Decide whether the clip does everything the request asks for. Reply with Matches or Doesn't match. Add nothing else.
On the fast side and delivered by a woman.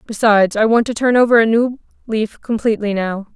Doesn't match